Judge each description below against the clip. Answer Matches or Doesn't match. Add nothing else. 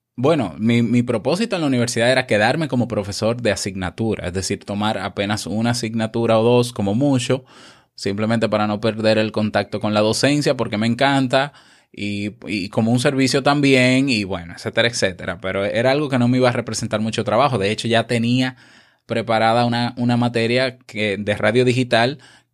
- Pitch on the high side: Doesn't match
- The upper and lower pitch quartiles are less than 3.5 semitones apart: Matches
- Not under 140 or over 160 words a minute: Doesn't match